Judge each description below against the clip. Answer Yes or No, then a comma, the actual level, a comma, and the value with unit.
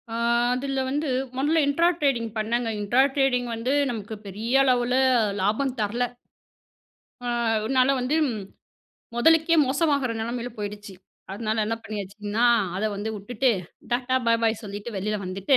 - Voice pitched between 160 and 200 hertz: No, high, 240 Hz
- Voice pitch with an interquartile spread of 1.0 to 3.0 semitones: No, average, 3.8 semitones